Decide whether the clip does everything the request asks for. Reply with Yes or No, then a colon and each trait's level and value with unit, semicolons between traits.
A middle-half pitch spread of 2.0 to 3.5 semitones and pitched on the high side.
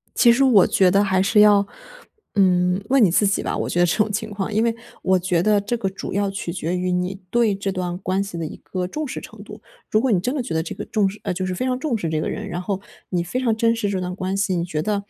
Yes: average, 3.0 semitones; high, 195 Hz